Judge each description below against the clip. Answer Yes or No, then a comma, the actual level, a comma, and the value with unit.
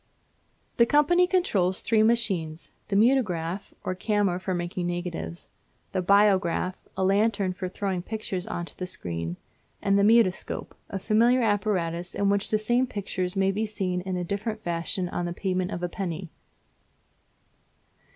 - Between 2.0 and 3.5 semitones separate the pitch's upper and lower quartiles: Yes, average, 3.1 semitones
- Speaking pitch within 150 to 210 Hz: Yes, high, 190 Hz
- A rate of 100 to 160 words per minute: Yes, average, 155 wpm